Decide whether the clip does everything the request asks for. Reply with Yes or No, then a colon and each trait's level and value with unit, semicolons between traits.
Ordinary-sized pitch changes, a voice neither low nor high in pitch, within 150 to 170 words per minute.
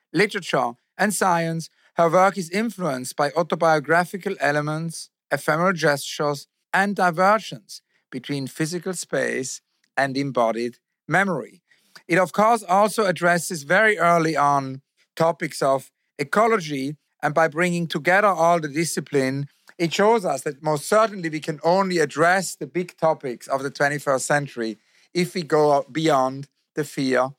No: average, 4.1 semitones; medium, 160 Hz; slow, 135 wpm